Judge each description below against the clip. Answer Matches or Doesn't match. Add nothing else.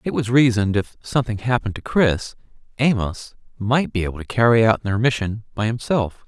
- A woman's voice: Doesn't match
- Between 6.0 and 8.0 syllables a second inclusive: Doesn't match